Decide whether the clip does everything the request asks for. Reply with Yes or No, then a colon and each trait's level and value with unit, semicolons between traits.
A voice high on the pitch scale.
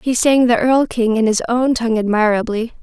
Yes: high, 235 Hz